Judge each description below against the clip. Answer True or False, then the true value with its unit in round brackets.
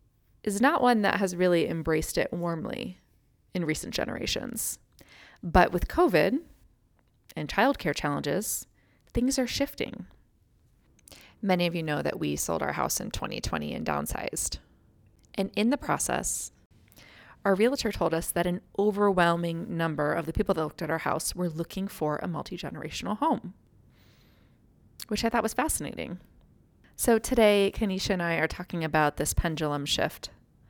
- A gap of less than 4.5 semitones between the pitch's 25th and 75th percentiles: False (5.0 semitones)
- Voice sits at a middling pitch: True (180 Hz)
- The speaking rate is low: False (150 wpm)